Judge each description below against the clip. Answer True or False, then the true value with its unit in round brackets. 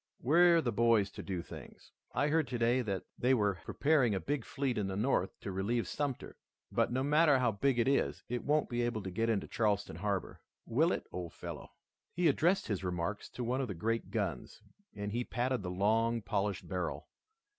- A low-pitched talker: True (115 Hz)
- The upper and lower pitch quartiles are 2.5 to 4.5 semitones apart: False (4.9 semitones)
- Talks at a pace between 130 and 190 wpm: False (200 wpm)